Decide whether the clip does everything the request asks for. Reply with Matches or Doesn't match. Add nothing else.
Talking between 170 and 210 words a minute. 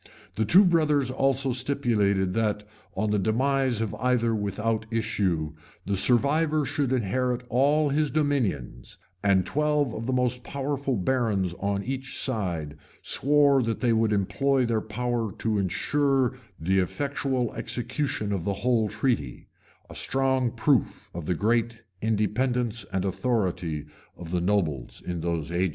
Doesn't match